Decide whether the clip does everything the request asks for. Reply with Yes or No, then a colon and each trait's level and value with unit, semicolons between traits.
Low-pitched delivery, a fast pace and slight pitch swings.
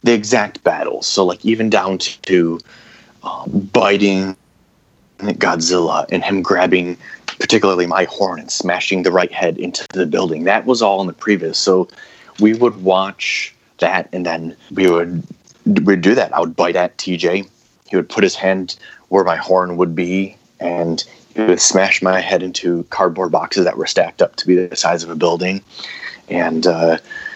No: very low, 95 Hz; average, 175 wpm; narrow, 2.1 semitones